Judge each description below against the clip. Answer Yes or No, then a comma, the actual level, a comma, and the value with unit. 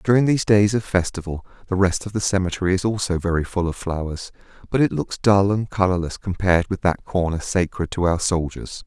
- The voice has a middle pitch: No, very low, 95 Hz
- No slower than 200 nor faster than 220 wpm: Yes, fast, 205 wpm